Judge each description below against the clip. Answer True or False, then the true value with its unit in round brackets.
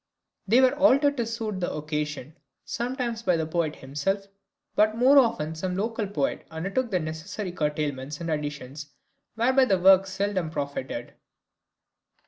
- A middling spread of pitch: False (6.9 semitones)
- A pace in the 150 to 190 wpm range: False (140 wpm)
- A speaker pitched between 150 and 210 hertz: True (185 Hz)